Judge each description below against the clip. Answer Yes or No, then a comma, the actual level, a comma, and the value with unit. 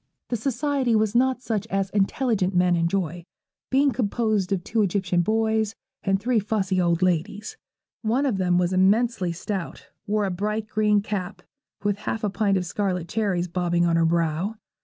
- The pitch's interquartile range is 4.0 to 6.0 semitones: No, average, 3.5 semitones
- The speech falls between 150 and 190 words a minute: Yes, average, 170 wpm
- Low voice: No, high, 200 Hz